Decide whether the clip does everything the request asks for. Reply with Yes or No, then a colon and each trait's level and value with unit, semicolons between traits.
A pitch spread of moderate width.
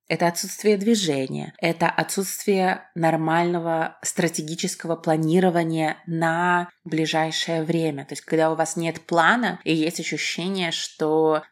No: narrow, 1.7 semitones